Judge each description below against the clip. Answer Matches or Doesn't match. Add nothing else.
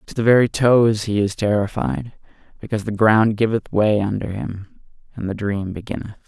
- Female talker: Doesn't match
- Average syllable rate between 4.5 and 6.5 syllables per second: Matches